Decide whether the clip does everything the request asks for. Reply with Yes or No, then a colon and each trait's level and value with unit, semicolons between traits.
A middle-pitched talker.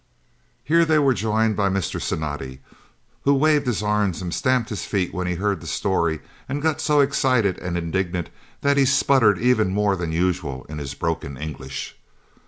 No: low, 100 Hz